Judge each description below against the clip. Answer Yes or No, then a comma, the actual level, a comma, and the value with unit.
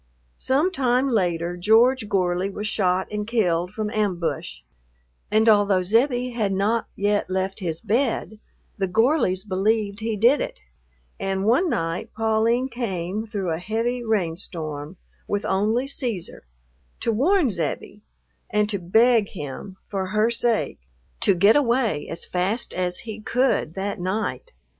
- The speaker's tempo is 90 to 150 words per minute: Yes, average, 140 wpm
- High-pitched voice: Yes, high, 210 Hz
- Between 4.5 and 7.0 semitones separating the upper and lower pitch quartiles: No, average, 4.0 semitones